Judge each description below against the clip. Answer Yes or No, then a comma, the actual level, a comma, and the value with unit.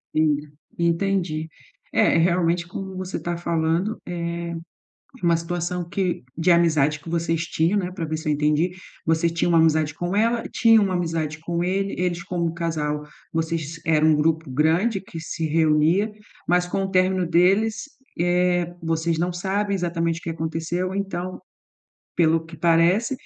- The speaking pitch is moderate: Yes, medium, 170 Hz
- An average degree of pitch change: No, narrow, 1.9 semitones